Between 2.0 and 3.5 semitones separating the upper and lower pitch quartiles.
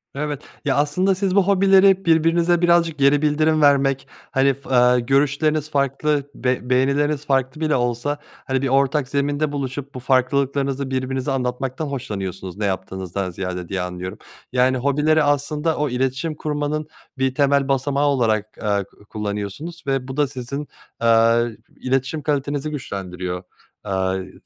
Yes: average, 3.2 semitones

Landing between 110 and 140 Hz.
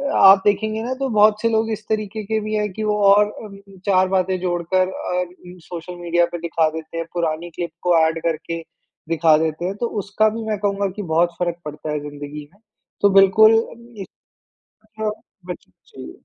No: medium, 185 Hz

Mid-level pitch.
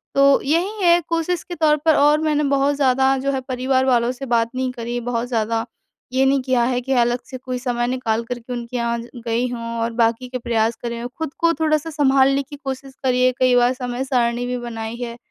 No: very high, 255 Hz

